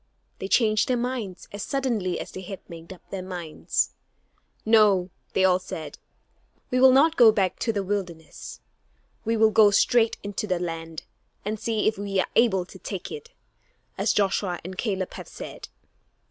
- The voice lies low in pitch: No, high, 200 Hz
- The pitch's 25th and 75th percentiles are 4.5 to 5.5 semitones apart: No, average, 3.5 semitones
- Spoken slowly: No, average, 175 wpm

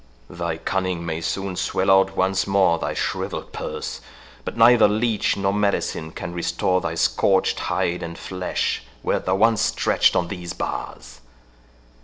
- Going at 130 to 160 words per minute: Yes, average, 150 wpm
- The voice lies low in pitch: Yes, very low, 95 Hz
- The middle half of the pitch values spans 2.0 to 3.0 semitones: Yes, narrow, 2.4 semitones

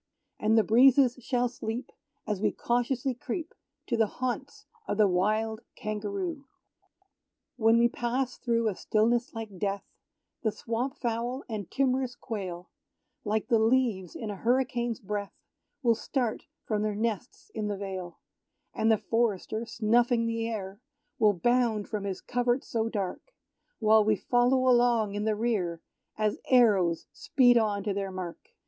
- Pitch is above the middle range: Yes, high, 225 Hz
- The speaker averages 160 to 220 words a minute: No, average, 150 wpm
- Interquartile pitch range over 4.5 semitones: No, average, 2.7 semitones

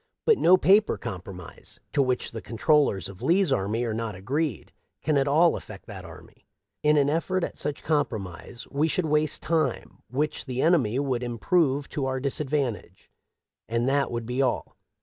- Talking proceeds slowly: No, average, 185 wpm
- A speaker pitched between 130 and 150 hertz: Yes, low, 135 Hz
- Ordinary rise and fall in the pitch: Yes, average, 4.7 semitones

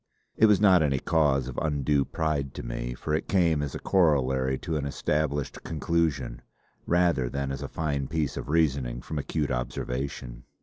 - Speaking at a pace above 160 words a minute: Yes, average, 175 wpm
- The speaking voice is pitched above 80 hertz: No, very low, 70 Hz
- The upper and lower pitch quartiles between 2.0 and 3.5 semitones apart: Yes, average, 3.2 semitones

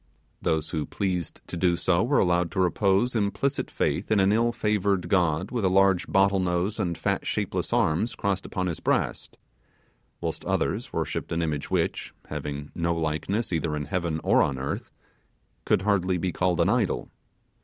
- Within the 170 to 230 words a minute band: Yes, average, 175 wpm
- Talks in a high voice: No, very low, 90 Hz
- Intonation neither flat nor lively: Yes, average, 3.0 semitones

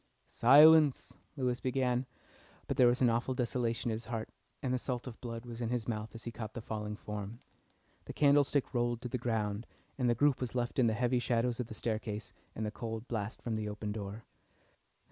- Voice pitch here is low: Yes, low, 120 Hz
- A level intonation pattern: Yes, narrow, 2.3 semitones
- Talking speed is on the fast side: Yes, fast, 210 wpm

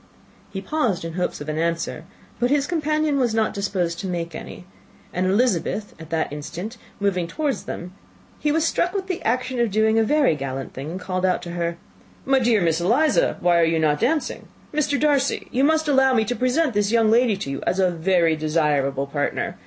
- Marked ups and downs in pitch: Yes, wide, 7.9 semitones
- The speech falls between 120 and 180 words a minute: No, fast, 205 wpm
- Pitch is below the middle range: No, high, 200 Hz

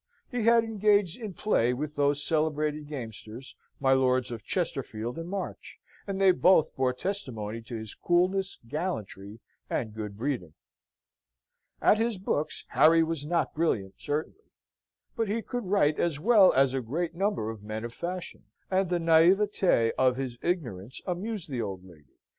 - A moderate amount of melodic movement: No, wide, 7.8 semitones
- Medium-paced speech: Yes, average, 160 wpm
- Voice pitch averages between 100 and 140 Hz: No, medium, 150 Hz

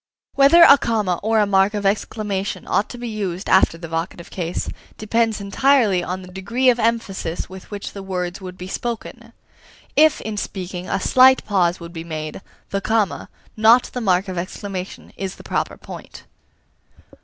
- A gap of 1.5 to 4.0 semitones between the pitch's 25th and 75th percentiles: Yes, average, 3.7 semitones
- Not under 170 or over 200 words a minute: Yes, average, 175 wpm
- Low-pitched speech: No, high, 195 Hz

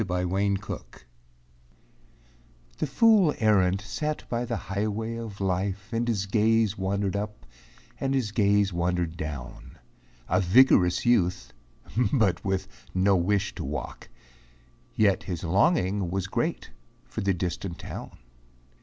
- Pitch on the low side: Yes, low, 100 Hz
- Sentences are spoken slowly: Yes, slow, 125 wpm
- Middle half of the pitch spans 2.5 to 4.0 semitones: Yes, average, 3.2 semitones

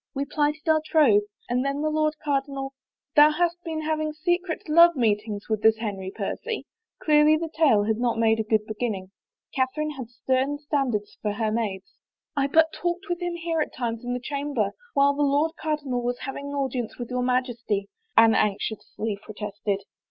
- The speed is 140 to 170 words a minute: No, average, 195 wpm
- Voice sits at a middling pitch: No, very high, 270 Hz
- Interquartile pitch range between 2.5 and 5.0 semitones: No, wide, 5.5 semitones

